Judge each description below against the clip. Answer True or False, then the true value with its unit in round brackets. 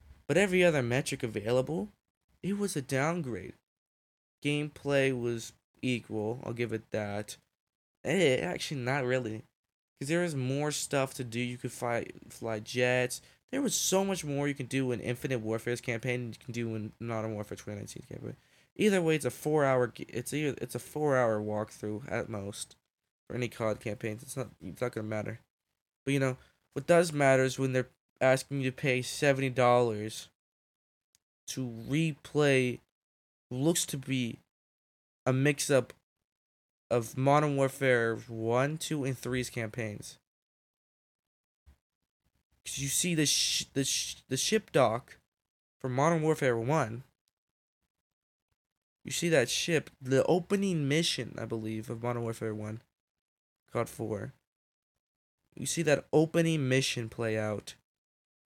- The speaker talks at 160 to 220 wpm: False (150 wpm)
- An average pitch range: True (3.8 semitones)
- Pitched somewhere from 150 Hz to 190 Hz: False (125 Hz)